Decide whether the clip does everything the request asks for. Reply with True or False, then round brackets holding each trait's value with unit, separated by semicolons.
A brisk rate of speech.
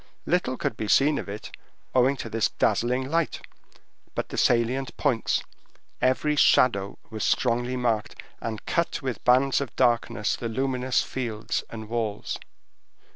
False (140 wpm)